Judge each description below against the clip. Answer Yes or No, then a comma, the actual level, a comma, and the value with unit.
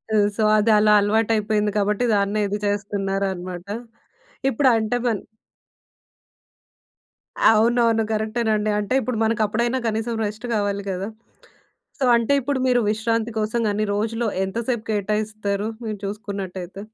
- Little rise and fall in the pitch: Yes, narrow, 2.0 semitones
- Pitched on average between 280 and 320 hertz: No, high, 215 Hz